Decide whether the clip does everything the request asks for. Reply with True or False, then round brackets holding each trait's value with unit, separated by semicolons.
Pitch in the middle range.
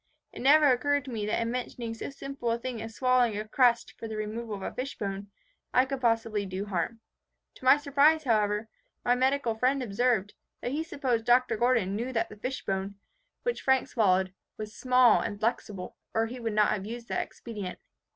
False (235 Hz)